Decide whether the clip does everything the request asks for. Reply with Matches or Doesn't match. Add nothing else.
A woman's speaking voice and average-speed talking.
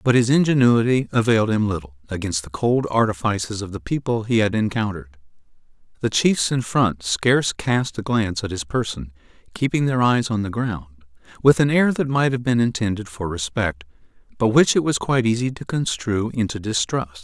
Doesn't match